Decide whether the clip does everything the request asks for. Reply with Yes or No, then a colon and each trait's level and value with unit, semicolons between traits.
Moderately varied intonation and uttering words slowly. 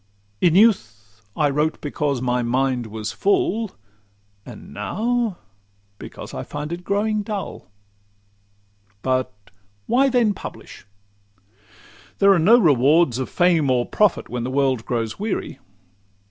No: wide, 8.8 semitones; slow, 120 wpm